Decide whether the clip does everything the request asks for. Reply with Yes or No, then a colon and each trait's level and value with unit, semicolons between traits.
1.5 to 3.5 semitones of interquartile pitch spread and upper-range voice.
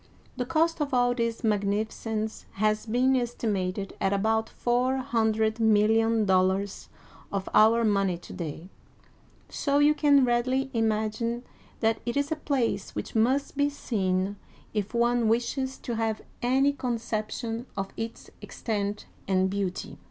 Yes: average, 3.2 semitones; high, 225 Hz